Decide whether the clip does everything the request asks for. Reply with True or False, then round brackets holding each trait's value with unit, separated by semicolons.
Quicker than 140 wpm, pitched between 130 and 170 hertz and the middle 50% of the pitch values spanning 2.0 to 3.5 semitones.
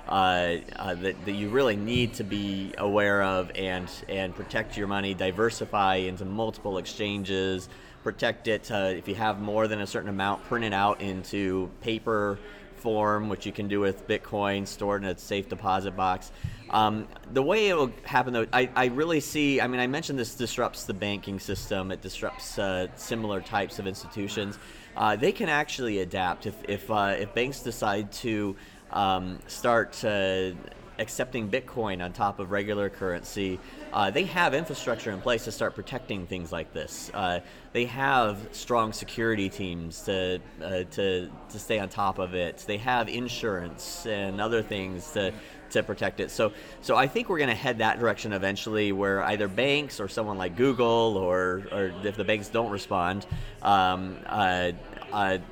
False (175 wpm; 100 Hz; 2.9 semitones)